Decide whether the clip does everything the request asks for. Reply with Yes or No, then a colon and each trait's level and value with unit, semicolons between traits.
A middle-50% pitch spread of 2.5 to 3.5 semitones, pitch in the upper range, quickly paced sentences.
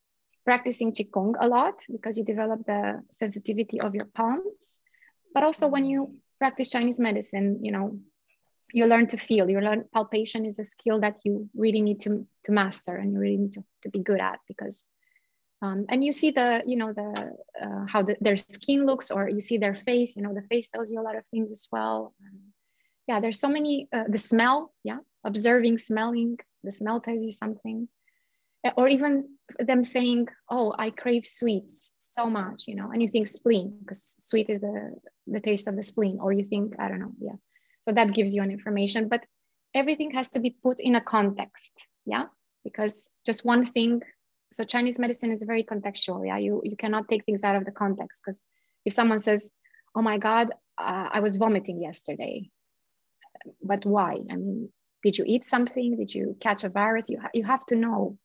Yes: average, 3.0 semitones; high, 220 Hz; fast, 200 wpm